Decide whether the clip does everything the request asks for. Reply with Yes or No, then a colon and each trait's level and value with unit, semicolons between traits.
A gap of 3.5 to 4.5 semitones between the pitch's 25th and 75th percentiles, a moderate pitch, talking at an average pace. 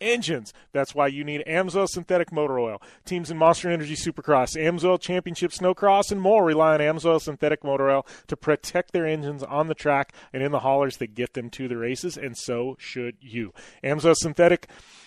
Yes: average, 4.1 semitones; medium, 150 Hz; average, 190 wpm